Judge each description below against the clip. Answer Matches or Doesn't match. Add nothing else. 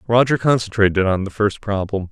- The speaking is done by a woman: Doesn't match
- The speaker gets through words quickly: Doesn't match